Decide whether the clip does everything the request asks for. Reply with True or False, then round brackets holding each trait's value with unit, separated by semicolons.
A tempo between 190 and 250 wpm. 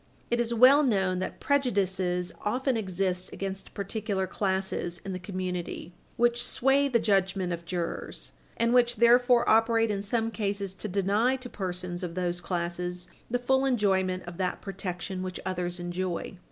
False (155 wpm)